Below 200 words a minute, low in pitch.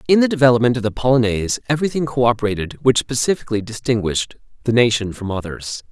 Yes: average, 160 wpm; low, 120 Hz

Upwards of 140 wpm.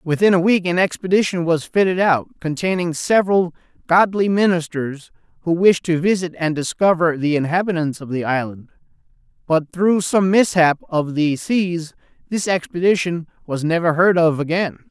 Yes: average, 150 wpm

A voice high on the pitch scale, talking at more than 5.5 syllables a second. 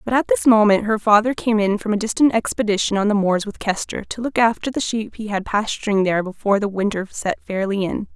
Yes: high, 210 Hz; 5.9 syllables/s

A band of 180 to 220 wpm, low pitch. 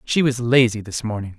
Yes: fast, 215 wpm; low, 115 Hz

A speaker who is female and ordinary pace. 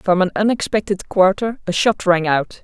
Yes: female; average, 180 wpm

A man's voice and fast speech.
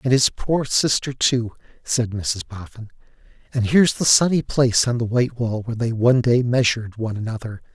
No: male; average, 185 wpm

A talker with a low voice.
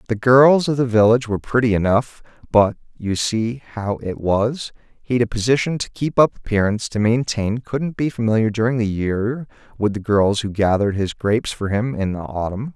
Yes: low, 115 Hz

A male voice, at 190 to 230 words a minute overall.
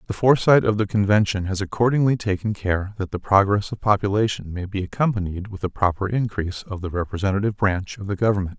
Yes: male; average, 195 wpm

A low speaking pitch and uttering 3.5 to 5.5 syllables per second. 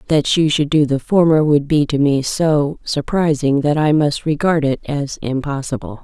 No: medium, 145 Hz; 4.6 syllables/s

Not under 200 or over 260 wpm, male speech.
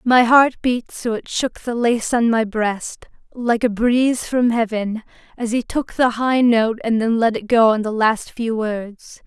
No: fast, 205 wpm; female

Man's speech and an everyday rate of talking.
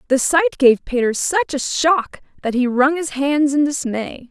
No: female; average, 195 wpm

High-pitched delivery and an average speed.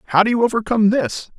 No: high, 215 Hz; fast, 215 wpm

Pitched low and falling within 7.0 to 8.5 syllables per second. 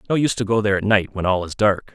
Yes: low, 105 Hz; 7.4 syllables/s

